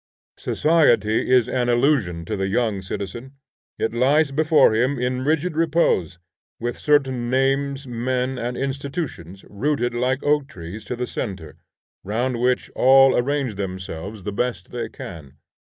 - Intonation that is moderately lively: Yes, average, 4.7 semitones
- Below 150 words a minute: Yes, average, 140 wpm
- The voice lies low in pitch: Yes, low, 125 Hz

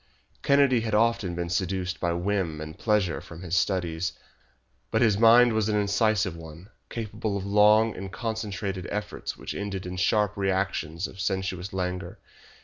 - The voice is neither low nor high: No, very low, 95 Hz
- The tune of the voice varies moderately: Yes, average, 3.0 semitones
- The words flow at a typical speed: Yes, average, 155 wpm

